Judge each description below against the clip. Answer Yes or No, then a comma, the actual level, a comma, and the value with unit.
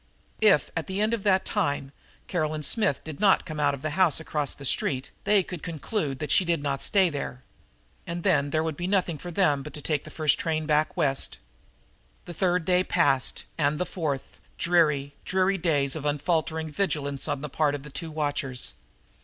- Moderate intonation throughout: Yes, average, 3.7 semitones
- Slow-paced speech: No, average, 200 wpm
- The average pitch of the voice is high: No, medium, 155 Hz